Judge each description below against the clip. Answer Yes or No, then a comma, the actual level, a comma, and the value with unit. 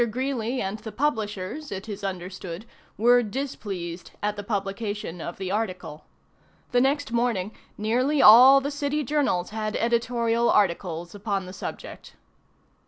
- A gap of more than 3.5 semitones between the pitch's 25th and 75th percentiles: Yes, average, 4.2 semitones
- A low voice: No, high, 215 Hz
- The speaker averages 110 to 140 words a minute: Yes, slow, 135 wpm